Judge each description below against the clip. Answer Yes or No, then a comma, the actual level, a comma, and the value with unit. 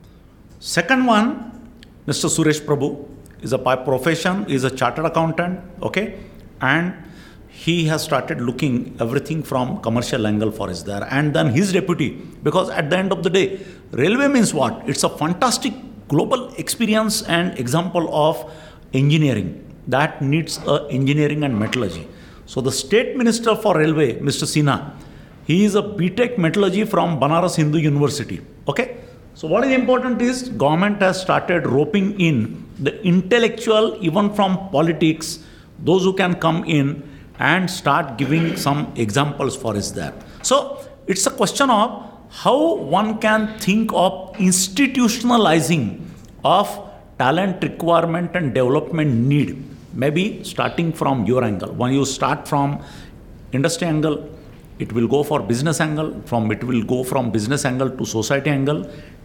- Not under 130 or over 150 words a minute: Yes, average, 145 wpm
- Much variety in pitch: Yes, wide, 5.7 semitones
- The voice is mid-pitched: Yes, medium, 160 Hz